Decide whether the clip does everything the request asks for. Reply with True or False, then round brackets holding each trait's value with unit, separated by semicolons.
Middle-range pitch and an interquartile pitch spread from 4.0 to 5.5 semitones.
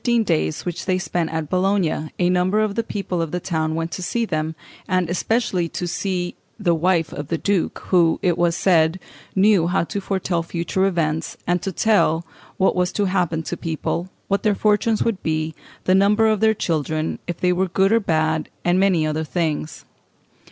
False (180 Hz; 3.2 semitones)